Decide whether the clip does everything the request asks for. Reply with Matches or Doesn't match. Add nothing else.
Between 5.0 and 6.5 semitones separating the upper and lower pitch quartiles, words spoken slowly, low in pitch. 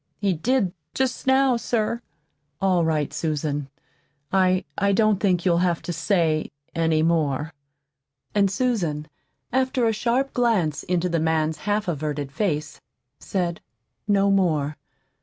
Doesn't match